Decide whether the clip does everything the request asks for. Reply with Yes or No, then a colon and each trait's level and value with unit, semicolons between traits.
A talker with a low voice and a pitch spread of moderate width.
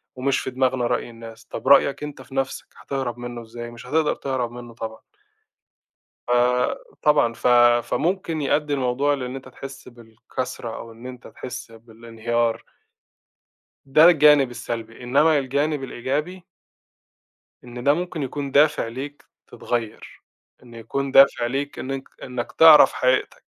Yes: low, 130 Hz; average, 3.1 semitones